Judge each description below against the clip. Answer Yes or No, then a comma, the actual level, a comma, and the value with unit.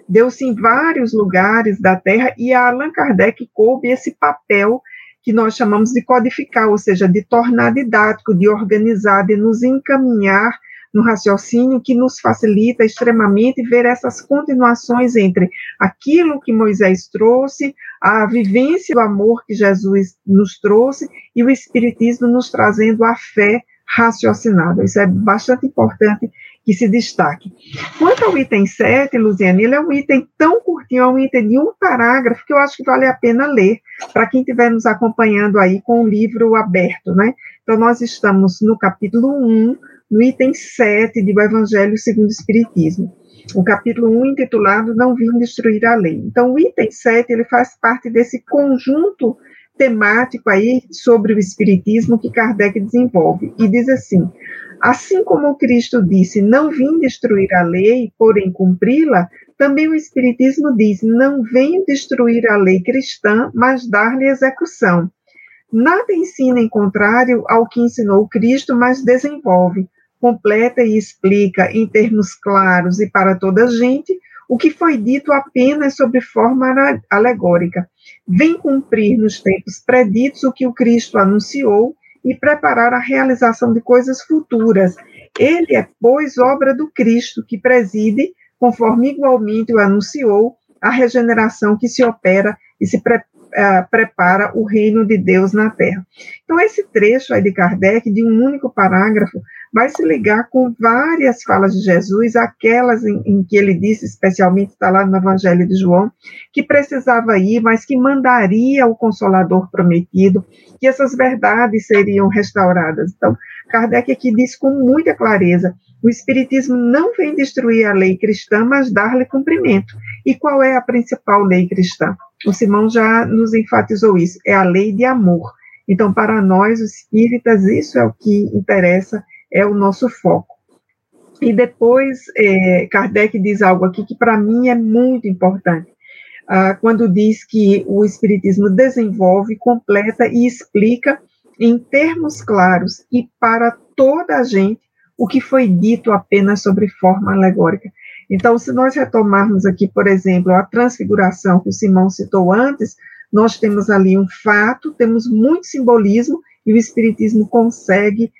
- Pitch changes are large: No, average, 3.9 semitones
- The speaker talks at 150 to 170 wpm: Yes, average, 155 wpm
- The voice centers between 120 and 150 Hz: No, high, 230 Hz